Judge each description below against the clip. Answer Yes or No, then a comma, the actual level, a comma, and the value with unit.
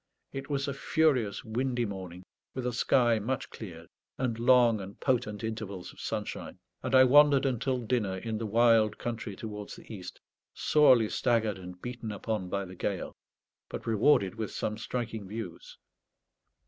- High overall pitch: No, low, 115 Hz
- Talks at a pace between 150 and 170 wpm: Yes, average, 160 wpm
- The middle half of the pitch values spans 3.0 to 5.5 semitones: Yes, average, 3.6 semitones